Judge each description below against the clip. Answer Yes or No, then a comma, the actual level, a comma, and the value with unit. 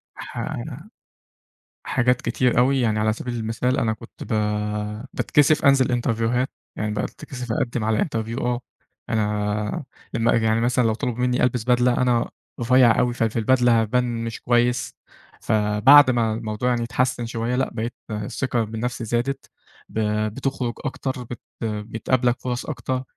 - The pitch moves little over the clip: Yes, narrow, 2.0 semitones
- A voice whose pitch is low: Yes, low, 120 Hz